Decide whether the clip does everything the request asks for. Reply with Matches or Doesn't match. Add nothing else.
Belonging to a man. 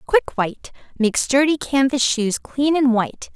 Doesn't match